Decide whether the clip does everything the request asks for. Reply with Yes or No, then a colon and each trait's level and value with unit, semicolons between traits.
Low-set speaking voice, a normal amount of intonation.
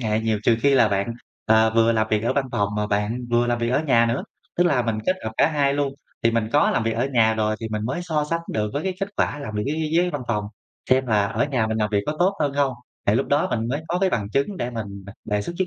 Yes: low, 115 Hz; average, 4.7 semitones